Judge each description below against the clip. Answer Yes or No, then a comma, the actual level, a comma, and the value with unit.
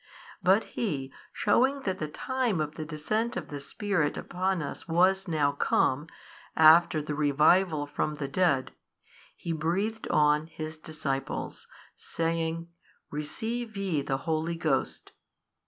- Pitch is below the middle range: No, medium, 160 Hz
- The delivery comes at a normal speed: No, slow, 130 wpm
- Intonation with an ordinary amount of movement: Yes, average, 4.1 semitones